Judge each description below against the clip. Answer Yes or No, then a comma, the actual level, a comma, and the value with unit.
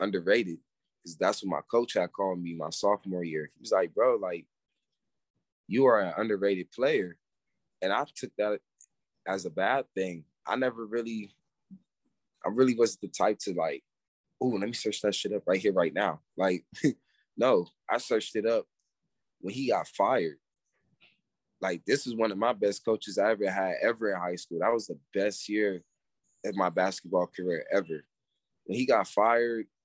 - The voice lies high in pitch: No, low, 105 Hz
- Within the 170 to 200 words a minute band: Yes, average, 180 wpm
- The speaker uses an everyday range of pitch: Yes, average, 3.9 semitones